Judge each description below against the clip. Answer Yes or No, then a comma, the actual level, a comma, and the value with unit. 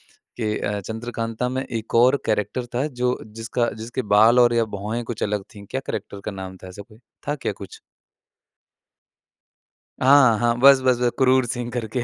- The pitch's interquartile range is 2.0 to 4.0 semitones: Yes, average, 2.8 semitones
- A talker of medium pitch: No, low, 120 Hz